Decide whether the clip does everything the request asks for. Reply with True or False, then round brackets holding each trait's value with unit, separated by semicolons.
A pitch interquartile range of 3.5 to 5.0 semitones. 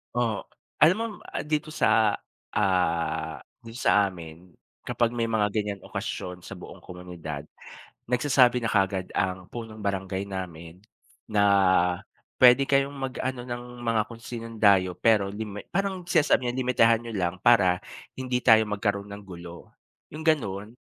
True (4.6 semitones)